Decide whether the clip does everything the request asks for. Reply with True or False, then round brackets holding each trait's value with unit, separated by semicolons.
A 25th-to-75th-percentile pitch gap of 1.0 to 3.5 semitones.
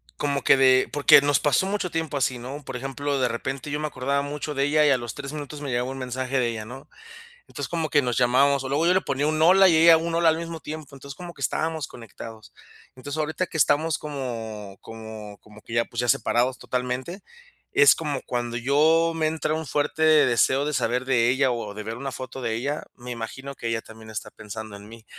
False (4.1 semitones)